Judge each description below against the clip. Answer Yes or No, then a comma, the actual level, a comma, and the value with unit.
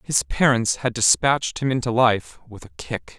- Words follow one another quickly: No, average, 190 wpm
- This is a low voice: Yes, low, 120 Hz